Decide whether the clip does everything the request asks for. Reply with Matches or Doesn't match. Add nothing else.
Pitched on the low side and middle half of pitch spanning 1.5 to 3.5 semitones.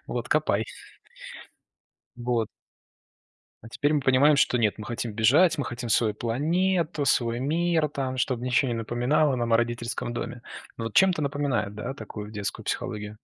Doesn't match